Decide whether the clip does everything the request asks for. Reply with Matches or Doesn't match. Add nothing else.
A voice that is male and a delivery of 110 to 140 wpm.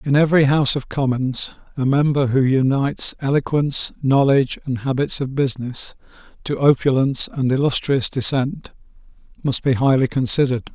Matches